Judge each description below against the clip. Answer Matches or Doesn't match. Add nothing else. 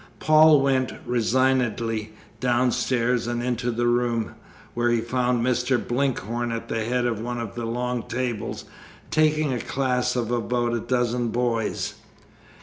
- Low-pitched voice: Matches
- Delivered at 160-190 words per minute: Doesn't match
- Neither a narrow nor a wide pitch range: Doesn't match